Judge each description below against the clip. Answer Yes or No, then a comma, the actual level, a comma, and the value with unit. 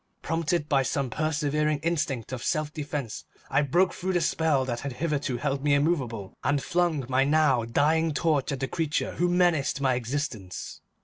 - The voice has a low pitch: No, medium, 145 Hz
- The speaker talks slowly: No, average, 175 wpm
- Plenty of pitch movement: No, average, 3.2 semitones